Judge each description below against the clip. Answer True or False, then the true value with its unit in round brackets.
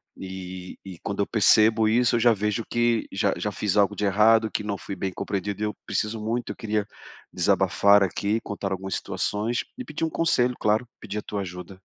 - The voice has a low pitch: True (105 Hz)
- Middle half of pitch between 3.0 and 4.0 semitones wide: False (2.5 semitones)